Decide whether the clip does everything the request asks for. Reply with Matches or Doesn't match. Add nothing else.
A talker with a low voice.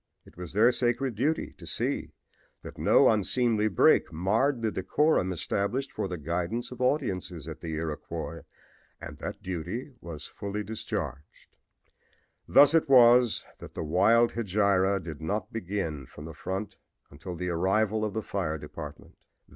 Matches